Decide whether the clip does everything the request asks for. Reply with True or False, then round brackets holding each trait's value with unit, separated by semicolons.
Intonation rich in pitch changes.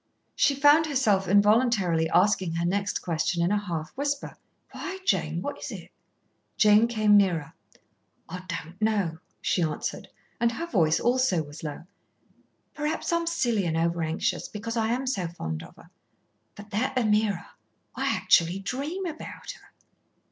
True (6.7 semitones)